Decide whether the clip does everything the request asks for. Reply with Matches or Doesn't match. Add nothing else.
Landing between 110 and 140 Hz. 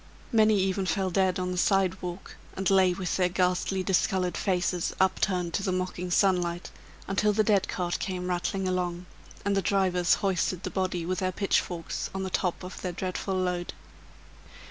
Doesn't match